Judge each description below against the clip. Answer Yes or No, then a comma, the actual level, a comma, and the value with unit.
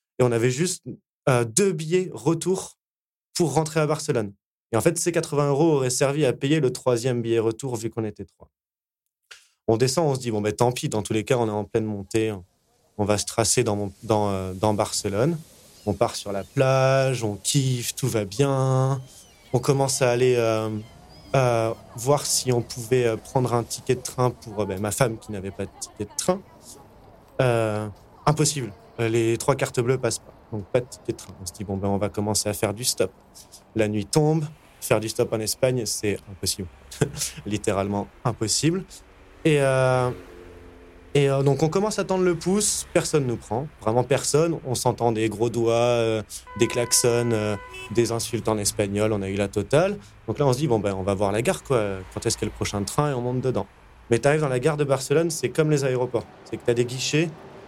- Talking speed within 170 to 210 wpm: No, fast, 220 wpm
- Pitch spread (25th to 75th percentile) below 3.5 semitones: No, average, 4.6 semitones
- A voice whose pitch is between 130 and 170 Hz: No, low, 120 Hz